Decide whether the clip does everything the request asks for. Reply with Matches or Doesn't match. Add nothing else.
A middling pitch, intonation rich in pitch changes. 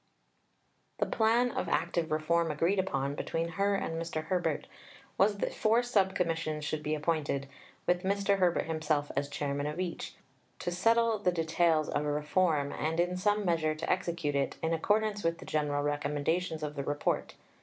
Doesn't match